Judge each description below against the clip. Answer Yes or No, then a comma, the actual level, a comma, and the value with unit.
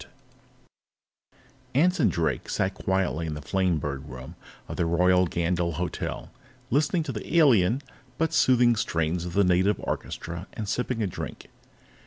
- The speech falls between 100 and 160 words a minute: Yes, average, 145 wpm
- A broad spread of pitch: Yes, wide, 5.9 semitones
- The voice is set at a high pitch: No, very low, 90 Hz